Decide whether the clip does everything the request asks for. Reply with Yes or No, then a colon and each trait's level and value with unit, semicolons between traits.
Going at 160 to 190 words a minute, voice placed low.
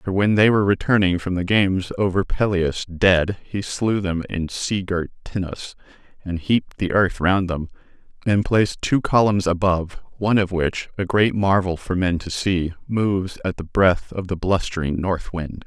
Yes: average, 185 wpm; very low, 95 Hz